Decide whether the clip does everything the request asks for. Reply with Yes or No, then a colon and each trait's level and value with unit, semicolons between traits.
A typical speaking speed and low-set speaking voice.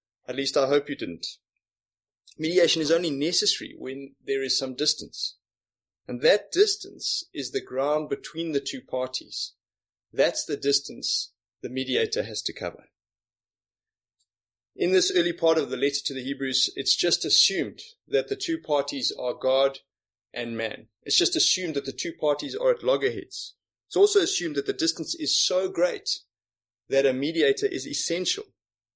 No: average, 160 wpm; medium, 150 Hz